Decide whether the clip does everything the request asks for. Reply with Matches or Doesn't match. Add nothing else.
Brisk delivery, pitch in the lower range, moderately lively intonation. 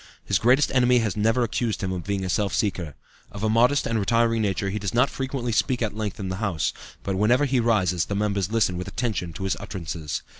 Matches